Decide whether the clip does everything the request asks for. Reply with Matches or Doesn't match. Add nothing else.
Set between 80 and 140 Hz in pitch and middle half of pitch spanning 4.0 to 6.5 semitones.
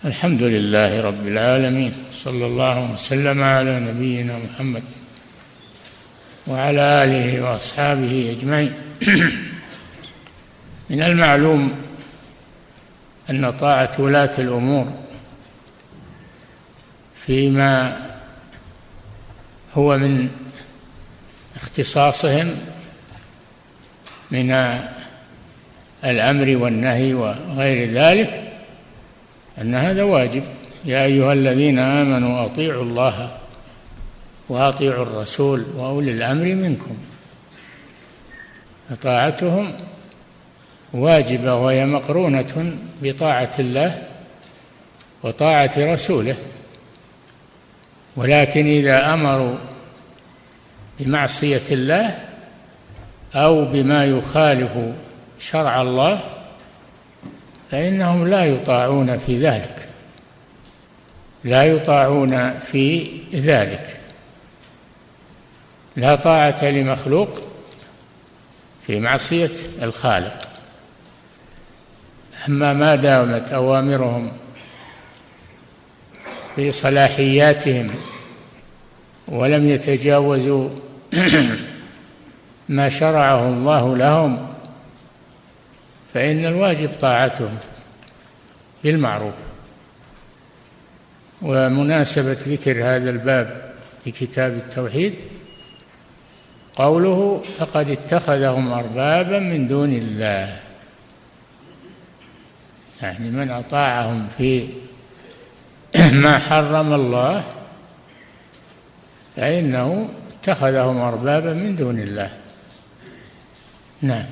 Doesn't match